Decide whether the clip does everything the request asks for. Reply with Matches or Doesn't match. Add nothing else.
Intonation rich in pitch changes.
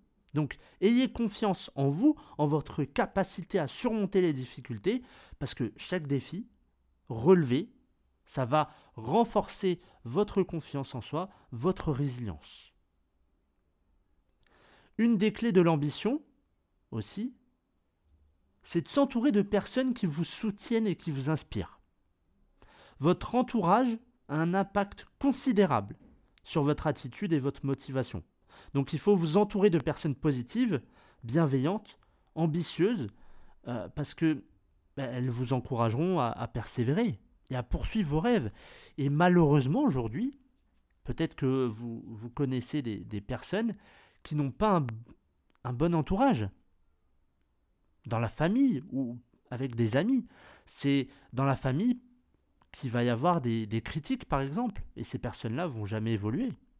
Matches